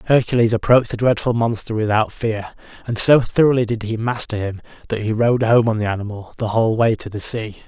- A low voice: Yes, low, 115 Hz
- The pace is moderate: No, fast, 210 wpm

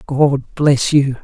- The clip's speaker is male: Yes, male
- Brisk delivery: No, average, 145 wpm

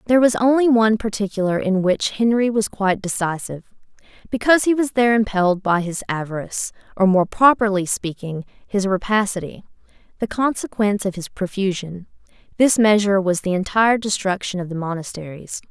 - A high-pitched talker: Yes, high, 200 Hz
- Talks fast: No, average, 150 wpm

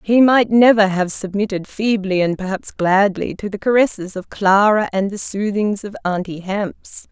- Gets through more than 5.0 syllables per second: No, 4.7 syllables/s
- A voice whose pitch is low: No, high, 200 Hz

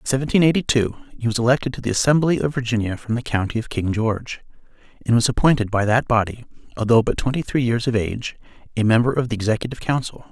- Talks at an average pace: No, fast, 215 wpm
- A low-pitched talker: Yes, low, 120 Hz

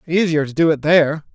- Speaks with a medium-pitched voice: Yes, medium, 155 Hz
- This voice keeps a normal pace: No, fast, 225 wpm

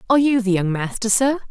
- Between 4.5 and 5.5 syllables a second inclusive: No, 6.5 syllables/s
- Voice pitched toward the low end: No, high, 225 Hz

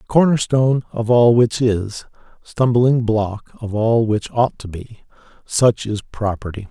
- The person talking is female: No, male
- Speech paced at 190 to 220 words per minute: No, average, 145 wpm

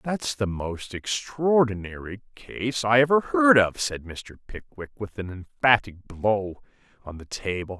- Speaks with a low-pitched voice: Yes, low, 110 Hz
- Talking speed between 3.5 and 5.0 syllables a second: Yes, 4.1 syllables/s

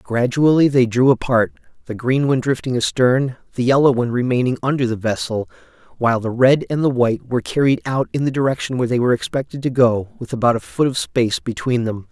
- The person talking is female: No, male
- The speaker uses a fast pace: Yes, fast, 210 wpm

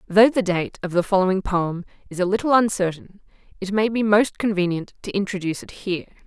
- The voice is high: Yes, high, 195 Hz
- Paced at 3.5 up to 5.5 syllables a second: No, 5.9 syllables/s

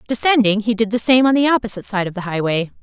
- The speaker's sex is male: No, female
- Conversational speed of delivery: No, fast, 255 wpm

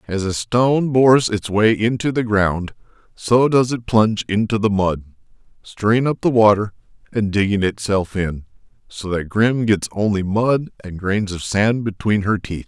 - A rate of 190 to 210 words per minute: No, average, 175 wpm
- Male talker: Yes, male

